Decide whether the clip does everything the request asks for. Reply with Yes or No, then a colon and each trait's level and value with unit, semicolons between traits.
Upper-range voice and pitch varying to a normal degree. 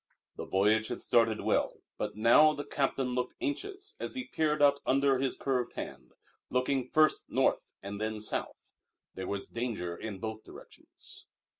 No: low, 125 Hz; average, 4.8 semitones